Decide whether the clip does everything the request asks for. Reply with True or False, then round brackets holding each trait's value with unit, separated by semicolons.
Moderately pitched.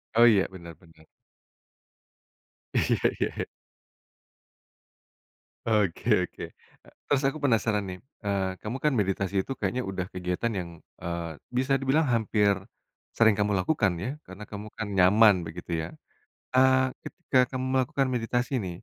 False (105 Hz)